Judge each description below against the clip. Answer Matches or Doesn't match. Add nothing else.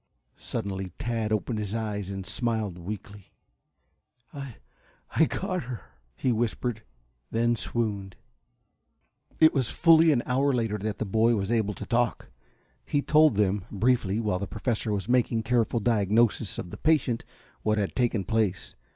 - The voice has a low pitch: Matches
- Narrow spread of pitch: Doesn't match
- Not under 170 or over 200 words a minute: Doesn't match